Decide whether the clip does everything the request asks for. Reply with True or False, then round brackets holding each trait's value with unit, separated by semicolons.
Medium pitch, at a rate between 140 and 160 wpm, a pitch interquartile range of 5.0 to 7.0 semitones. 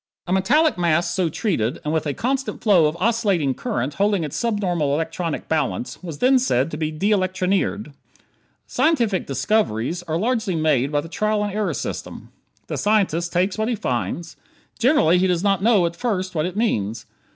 False (180 Hz; 180 wpm; 5.4 semitones)